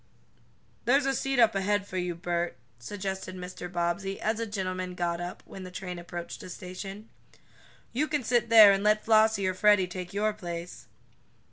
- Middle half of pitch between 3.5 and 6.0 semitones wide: No, average, 3.1 semitones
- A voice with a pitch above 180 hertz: Yes, high, 190 Hz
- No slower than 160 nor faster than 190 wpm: Yes, average, 175 wpm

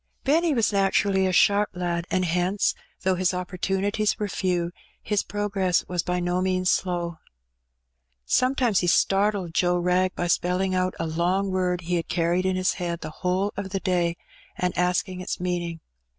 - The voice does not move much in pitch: Yes, narrow, 1.6 semitones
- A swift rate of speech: No, average, 170 wpm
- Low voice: No, medium, 185 Hz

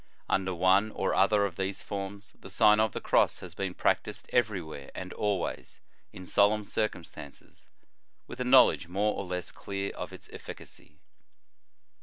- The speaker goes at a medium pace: Yes, average, 160 wpm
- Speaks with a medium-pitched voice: No, low, 100 Hz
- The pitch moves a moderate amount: No, narrow, 2.3 semitones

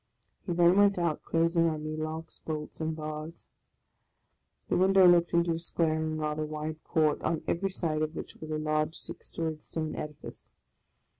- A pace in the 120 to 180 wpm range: Yes, average, 175 wpm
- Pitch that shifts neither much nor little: No, narrow, 1.7 semitones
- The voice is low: No, medium, 160 Hz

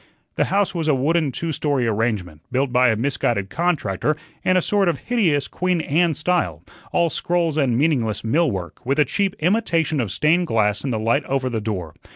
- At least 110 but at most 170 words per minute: No, average, 195 wpm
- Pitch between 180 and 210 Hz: No, medium, 140 Hz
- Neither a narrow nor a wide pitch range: No, wide, 6.8 semitones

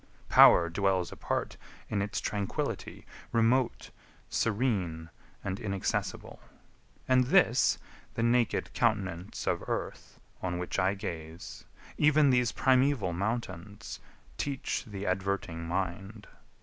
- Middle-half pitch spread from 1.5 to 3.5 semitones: No, average, 4.3 semitones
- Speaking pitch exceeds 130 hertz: No, low, 100 Hz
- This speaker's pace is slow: Yes, slow, 105 wpm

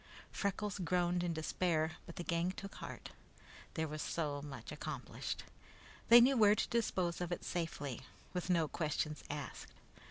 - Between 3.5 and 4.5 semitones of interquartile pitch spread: No, average, 2.9 semitones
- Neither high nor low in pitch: Yes, medium, 170 Hz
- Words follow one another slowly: No, average, 155 wpm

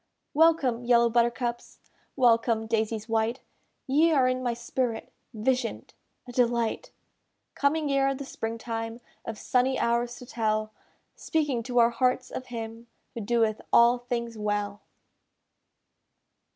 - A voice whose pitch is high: Yes, high, 235 Hz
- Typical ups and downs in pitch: No, narrow, 2.0 semitones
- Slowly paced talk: Yes, slow, 125 wpm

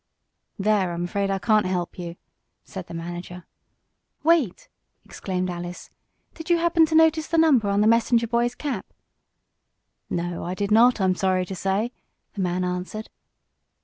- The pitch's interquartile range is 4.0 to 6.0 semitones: Yes, average, 4.9 semitones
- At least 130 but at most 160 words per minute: Yes, average, 155 wpm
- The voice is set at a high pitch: Yes, high, 195 Hz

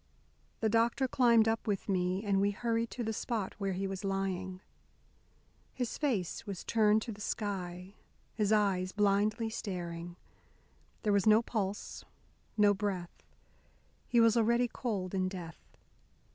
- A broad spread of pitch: No, average, 3.1 semitones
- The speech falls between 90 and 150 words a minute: Yes, average, 145 wpm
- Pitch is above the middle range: Yes, high, 205 Hz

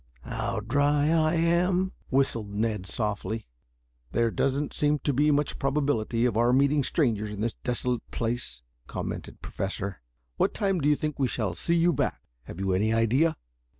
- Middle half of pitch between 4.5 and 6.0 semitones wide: Yes, average, 5.3 semitones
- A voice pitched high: No, low, 125 Hz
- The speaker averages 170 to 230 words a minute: Yes, average, 175 wpm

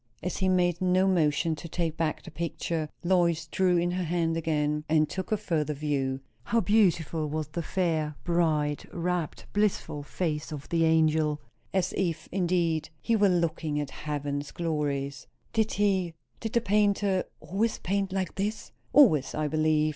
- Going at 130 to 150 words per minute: No, average, 160 wpm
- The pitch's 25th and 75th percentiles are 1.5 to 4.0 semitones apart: Yes, average, 3.5 semitones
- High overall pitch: No, medium, 165 Hz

